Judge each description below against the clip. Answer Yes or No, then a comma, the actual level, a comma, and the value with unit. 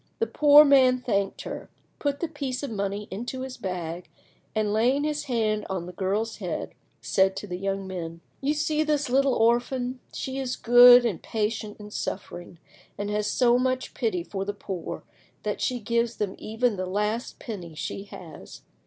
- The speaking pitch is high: Yes, high, 225 Hz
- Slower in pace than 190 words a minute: Yes, average, 180 wpm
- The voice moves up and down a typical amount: Yes, average, 4.7 semitones